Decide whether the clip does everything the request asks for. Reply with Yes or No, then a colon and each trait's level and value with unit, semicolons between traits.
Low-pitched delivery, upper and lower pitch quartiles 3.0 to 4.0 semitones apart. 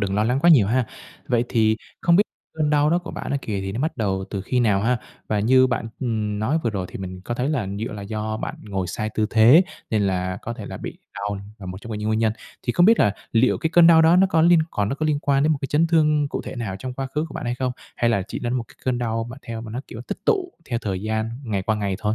No: low, 115 Hz; average, 5.0 semitones